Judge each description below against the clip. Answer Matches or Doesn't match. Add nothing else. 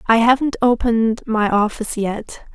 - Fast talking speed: Doesn't match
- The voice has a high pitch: Matches